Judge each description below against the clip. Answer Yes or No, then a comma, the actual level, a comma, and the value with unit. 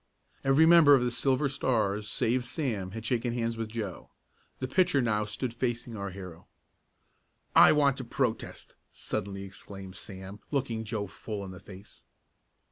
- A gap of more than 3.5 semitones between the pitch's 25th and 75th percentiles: Yes, average, 4.5 semitones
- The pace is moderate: Yes, average, 155 wpm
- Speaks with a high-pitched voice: No, low, 115 Hz